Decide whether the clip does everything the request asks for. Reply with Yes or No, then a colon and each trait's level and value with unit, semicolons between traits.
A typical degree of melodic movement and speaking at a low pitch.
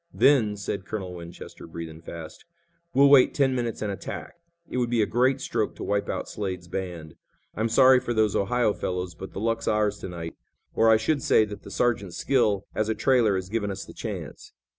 Yes: average, 4.2 semitones; low, 105 Hz